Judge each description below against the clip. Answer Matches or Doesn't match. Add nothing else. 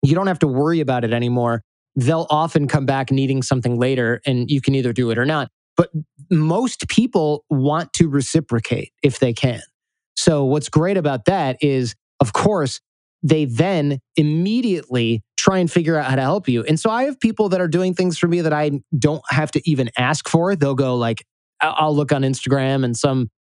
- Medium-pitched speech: Matches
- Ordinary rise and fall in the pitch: Matches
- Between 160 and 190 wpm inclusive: Doesn't match